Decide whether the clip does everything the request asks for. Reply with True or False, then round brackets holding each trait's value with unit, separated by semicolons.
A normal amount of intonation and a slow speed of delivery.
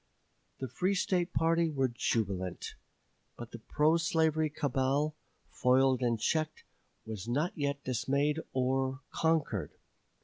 True (3.9 semitones; 115 wpm)